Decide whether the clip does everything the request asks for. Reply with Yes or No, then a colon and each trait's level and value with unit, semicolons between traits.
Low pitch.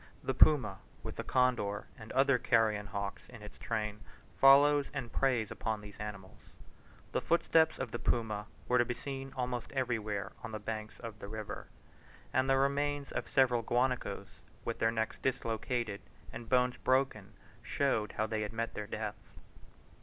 Yes: low, 115 Hz